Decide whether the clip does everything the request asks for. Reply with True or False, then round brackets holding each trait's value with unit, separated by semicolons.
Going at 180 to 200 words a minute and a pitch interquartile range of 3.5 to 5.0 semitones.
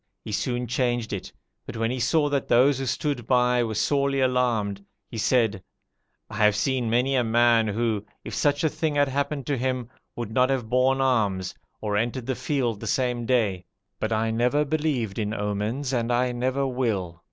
False (190 wpm; 3.1 semitones)